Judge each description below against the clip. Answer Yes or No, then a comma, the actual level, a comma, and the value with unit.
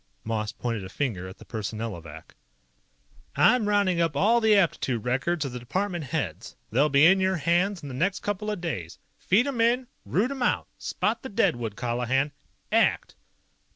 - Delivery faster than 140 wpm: Yes, average, 175 wpm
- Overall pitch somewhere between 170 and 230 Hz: No, medium, 155 Hz